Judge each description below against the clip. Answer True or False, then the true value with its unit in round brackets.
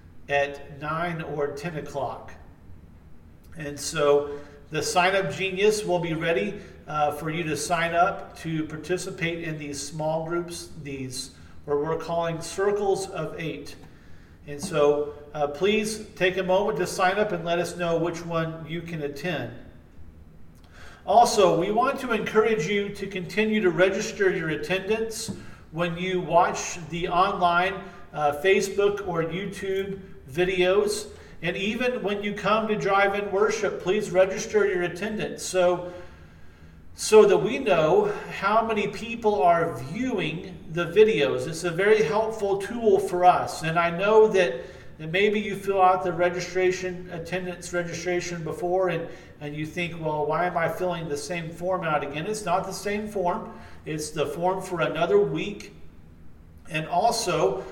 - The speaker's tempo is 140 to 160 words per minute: True (150 wpm)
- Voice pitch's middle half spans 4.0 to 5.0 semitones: True (4.5 semitones)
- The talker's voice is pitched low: False (175 Hz)